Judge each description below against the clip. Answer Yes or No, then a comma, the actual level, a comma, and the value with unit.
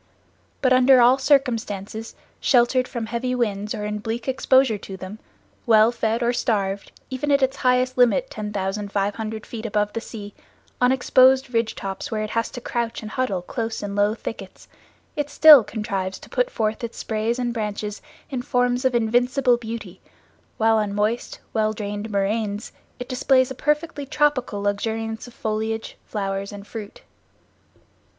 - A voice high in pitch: Yes, high, 225 Hz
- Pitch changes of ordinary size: Yes, average, 3.3 semitones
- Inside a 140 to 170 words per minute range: Yes, average, 160 wpm